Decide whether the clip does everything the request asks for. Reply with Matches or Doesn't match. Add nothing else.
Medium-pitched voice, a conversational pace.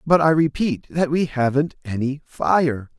Matches